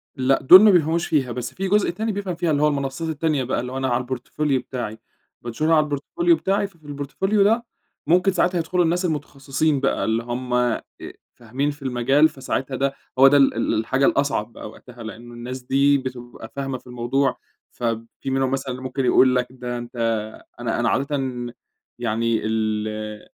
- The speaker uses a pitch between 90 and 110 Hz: No, low, 135 Hz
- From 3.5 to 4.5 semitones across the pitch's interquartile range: Yes, average, 4.1 semitones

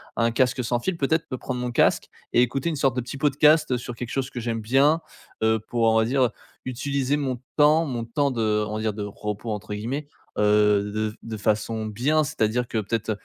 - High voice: No, low, 120 Hz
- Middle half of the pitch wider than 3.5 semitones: Yes, average, 3.9 semitones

